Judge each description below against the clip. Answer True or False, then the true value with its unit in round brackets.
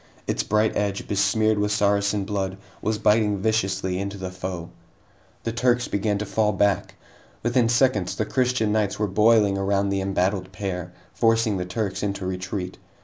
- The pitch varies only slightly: True (2.2 semitones)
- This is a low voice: True (100 Hz)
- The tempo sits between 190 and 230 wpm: False (160 wpm)